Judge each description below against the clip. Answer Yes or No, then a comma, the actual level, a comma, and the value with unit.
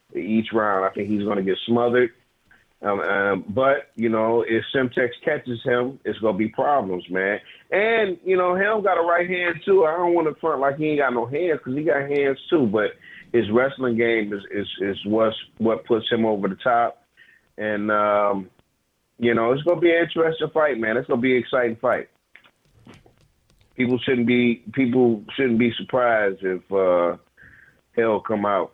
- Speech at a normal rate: Yes, average, 195 wpm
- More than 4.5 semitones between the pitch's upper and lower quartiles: Yes, wide, 5.4 semitones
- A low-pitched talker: Yes, low, 120 Hz